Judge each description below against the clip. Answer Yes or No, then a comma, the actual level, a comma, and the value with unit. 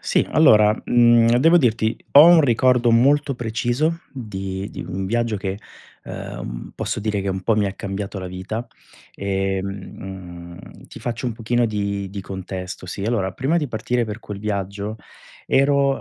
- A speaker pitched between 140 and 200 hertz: No, low, 105 Hz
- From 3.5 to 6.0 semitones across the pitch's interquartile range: Yes, average, 3.9 semitones